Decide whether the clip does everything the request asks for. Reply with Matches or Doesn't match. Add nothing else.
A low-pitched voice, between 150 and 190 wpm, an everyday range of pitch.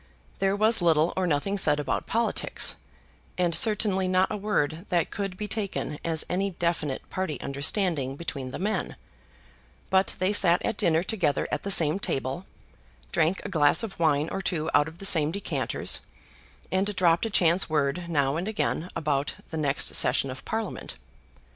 Doesn't match